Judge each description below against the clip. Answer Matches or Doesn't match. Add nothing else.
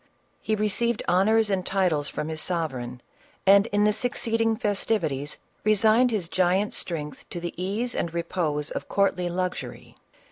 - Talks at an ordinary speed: Matches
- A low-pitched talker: Doesn't match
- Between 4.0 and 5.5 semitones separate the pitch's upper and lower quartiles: Matches